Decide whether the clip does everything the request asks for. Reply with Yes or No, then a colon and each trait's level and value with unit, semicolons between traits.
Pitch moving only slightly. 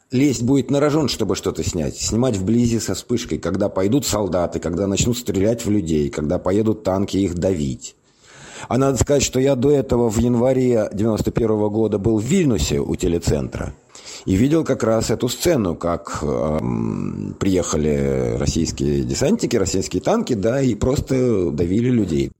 No: wide, 5.6 semitones